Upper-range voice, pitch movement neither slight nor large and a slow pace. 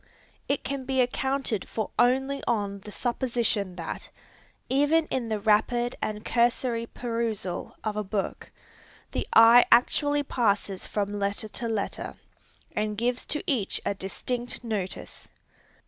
Yes: high, 230 Hz; average, 3.3 semitones; slow, 130 wpm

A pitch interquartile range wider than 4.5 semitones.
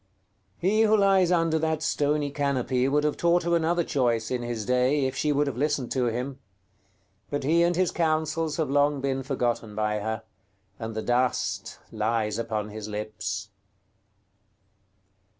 Yes: wide, 5.4 semitones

